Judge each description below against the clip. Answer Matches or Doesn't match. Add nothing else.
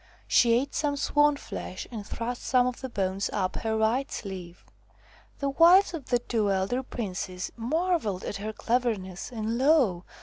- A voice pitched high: Matches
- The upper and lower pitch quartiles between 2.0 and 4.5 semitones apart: Doesn't match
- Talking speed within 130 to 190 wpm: Matches